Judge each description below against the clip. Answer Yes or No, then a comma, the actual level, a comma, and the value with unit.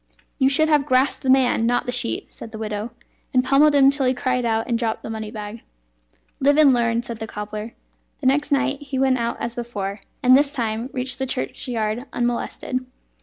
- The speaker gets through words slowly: No, fast, 205 wpm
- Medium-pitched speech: No, high, 245 Hz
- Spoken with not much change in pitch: No, average, 3.2 semitones